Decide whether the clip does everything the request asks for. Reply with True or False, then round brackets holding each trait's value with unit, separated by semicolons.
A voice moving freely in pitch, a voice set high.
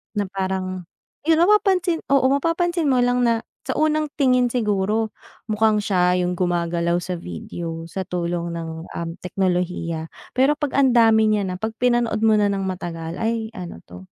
True (5.8 semitones; 205 Hz)